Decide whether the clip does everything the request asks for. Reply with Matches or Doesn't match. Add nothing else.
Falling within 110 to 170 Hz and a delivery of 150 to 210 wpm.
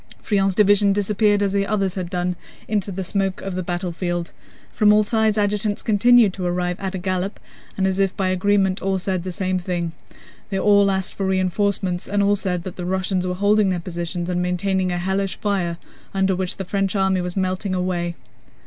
Doesn't match